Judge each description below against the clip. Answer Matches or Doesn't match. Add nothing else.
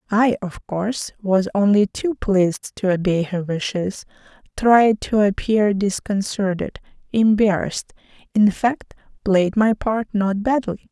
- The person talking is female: Matches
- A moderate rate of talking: Doesn't match